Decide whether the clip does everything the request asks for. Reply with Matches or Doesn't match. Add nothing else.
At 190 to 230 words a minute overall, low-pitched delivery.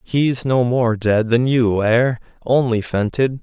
Doesn't match